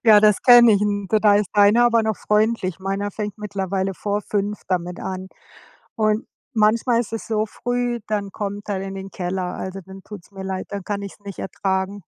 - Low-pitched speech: No, high, 205 Hz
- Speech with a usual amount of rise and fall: No, narrow, 1.9 semitones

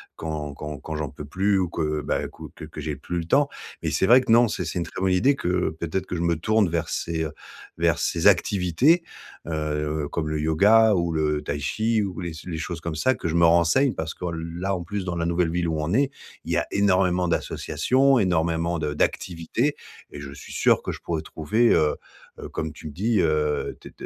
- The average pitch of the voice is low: Yes, very low, 85 Hz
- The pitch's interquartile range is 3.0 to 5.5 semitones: Yes, average, 3.8 semitones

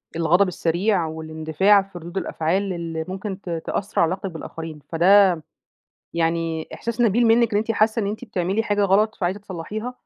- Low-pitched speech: No, high, 190 Hz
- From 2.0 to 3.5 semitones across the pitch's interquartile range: No, average, 3.9 semitones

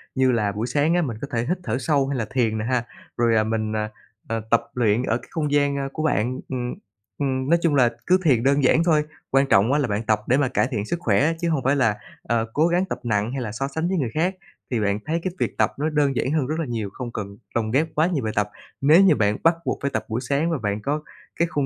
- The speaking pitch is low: Yes, low, 130 Hz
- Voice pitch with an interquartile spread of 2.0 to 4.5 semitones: No, average, 5.1 semitones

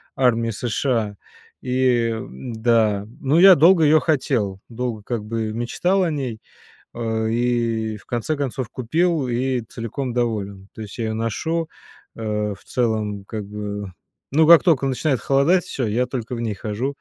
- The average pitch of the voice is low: Yes, low, 120 Hz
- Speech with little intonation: No, average, 3.7 semitones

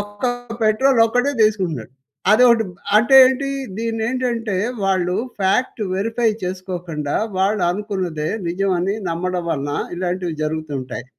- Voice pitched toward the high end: Yes, high, 195 Hz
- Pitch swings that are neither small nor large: Yes, average, 4.5 semitones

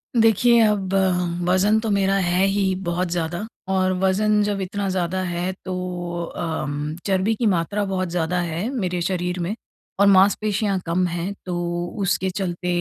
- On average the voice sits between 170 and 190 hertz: Yes, medium, 185 Hz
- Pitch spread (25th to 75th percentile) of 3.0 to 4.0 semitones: No, narrow, 2.4 semitones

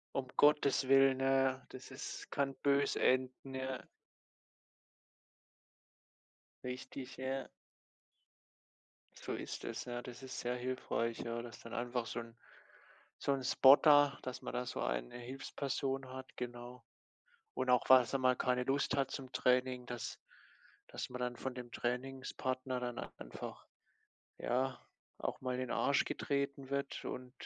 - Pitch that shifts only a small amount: Yes, narrow, 1.5 semitones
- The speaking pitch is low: Yes, low, 130 Hz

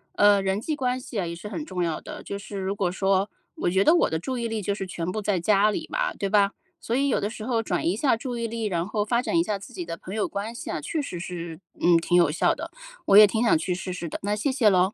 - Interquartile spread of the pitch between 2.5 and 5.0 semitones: Yes, average, 4.0 semitones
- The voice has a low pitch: No, high, 200 Hz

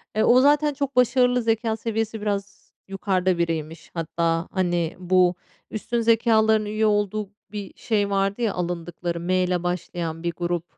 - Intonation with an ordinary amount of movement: Yes, average, 4.2 semitones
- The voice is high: Yes, high, 200 Hz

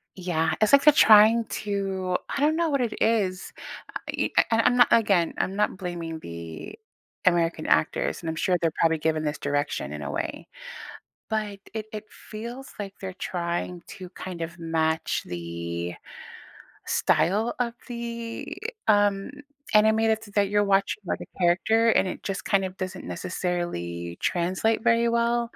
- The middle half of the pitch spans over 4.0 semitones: Yes, average, 5.0 semitones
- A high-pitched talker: Yes, high, 195 Hz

